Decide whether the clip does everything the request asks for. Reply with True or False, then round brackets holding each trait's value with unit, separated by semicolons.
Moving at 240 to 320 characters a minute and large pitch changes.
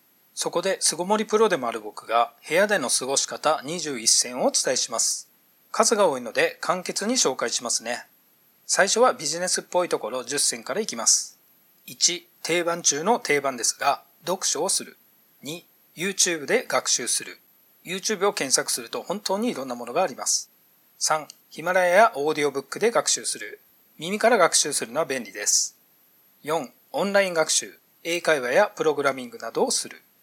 False (340 characters per minute; 5.8 semitones)